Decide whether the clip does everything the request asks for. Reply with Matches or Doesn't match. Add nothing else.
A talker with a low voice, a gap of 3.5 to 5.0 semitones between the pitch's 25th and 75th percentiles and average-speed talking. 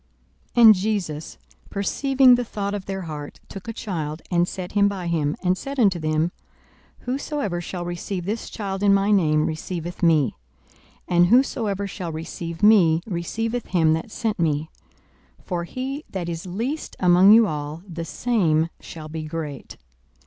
Doesn't match